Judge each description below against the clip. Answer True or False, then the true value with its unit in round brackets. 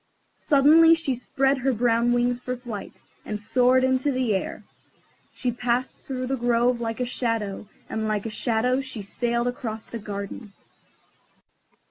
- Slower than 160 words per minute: True (150 wpm)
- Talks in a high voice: True (245 Hz)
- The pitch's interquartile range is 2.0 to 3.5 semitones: True (2.4 semitones)